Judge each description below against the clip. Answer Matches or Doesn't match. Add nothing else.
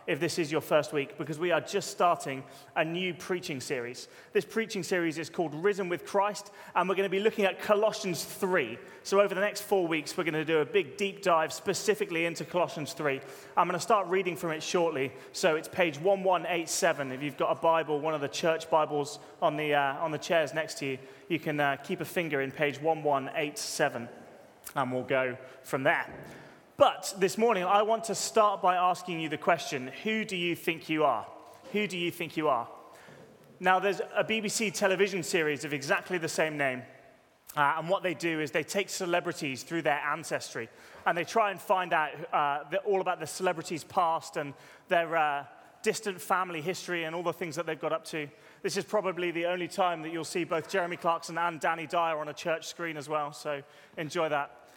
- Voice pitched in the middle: Matches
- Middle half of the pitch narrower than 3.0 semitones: Doesn't match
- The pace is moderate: Doesn't match